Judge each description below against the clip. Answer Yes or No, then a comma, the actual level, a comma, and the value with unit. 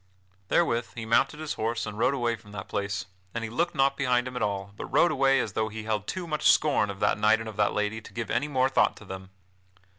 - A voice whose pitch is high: No, low, 115 Hz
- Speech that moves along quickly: Yes, fast, 260 wpm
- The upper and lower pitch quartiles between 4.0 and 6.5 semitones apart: Yes, average, 4.4 semitones